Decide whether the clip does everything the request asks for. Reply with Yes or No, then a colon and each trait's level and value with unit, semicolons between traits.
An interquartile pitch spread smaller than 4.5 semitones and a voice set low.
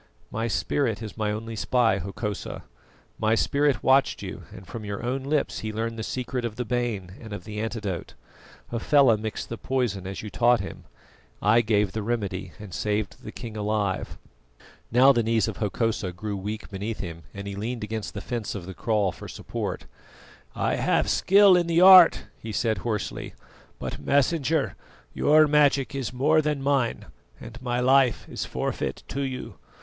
Yes: average, 3.8 semitones; low, 115 Hz